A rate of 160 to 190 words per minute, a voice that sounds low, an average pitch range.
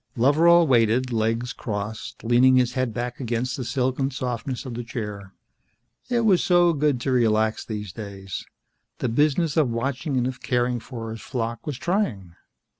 Yes: average, 165 wpm; low, 125 Hz; average, 3.3 semitones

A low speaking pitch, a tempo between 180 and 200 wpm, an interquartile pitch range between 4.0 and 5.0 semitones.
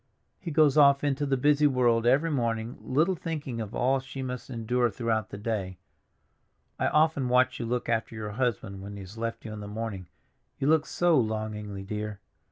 Yes: low, 120 Hz; average, 190 wpm; average, 4.3 semitones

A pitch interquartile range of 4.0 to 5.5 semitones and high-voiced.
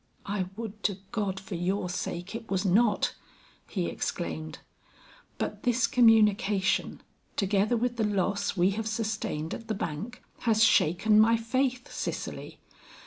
No: average, 3.0 semitones; high, 210 Hz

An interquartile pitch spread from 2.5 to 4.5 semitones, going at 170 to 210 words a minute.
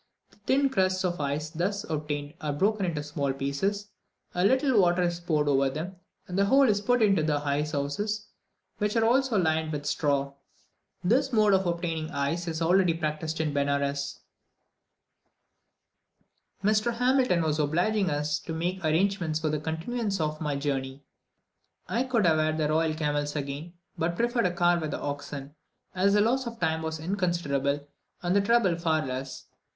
No: average, 5.2 semitones; average, 175 wpm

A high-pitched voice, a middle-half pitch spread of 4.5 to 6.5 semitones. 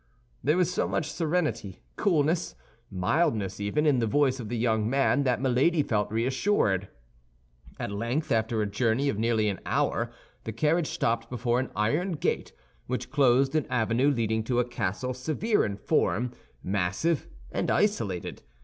No: low, 125 Hz; average, 5.3 semitones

